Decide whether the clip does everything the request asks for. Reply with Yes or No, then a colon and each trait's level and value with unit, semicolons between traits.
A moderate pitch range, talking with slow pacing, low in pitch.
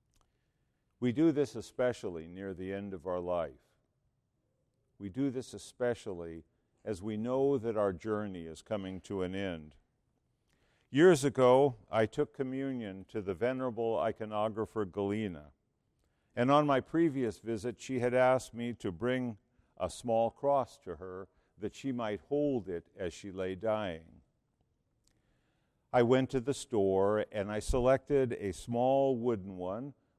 No: average, 4.9 semitones; average, 145 wpm; low, 110 Hz